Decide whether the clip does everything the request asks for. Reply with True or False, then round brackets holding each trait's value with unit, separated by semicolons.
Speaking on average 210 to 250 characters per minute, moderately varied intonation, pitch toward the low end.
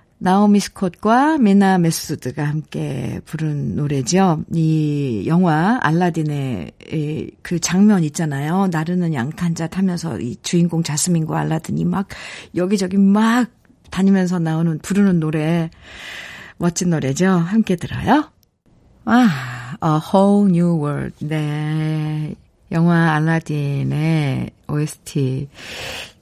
False (245 characters per minute; 3.7 semitones; 165 Hz)